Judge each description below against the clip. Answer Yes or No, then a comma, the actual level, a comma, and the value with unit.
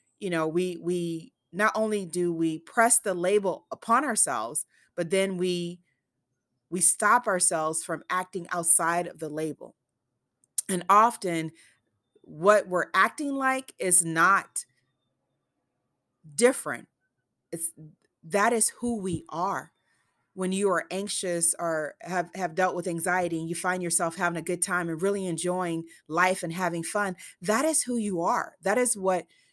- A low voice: No, medium, 180 Hz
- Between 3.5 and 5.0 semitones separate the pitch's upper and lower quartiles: No, average, 3.0 semitones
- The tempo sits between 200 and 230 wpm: No, average, 150 wpm